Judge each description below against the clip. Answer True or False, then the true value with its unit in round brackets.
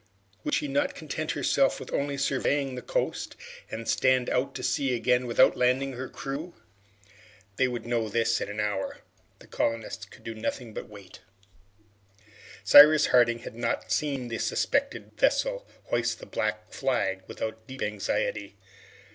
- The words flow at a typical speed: True (155 wpm)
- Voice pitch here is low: True (125 Hz)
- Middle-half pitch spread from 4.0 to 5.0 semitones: False (3.6 semitones)